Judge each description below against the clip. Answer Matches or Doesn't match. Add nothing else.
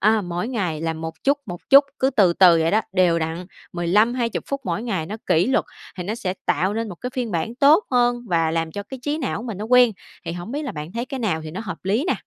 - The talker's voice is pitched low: Doesn't match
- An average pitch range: Doesn't match